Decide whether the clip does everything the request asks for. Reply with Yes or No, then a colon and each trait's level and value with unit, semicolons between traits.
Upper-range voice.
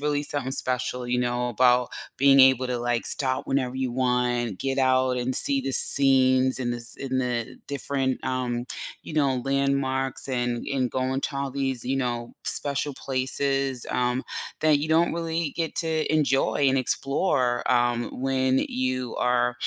No: low, 130 Hz